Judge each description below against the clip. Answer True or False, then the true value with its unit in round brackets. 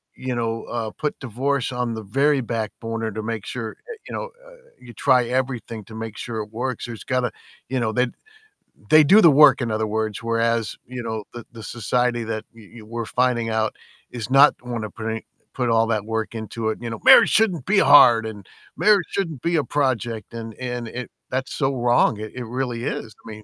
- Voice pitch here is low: True (120 Hz)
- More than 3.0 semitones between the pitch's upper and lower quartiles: False (2.5 semitones)